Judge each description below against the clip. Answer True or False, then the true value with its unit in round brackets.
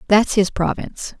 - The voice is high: True (200 Hz)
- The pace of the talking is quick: False (150 wpm)